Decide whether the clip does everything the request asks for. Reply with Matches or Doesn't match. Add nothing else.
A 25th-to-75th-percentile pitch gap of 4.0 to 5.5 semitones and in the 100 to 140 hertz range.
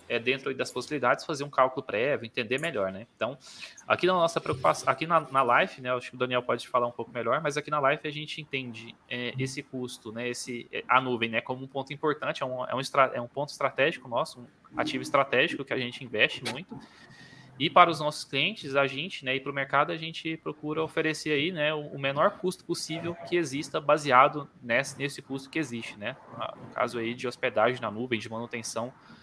Doesn't match